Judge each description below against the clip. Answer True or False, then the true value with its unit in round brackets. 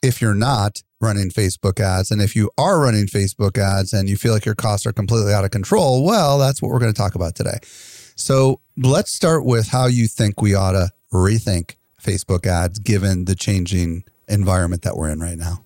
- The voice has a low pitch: True (105 Hz)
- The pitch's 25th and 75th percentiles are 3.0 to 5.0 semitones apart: True (3.5 semitones)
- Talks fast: True (210 wpm)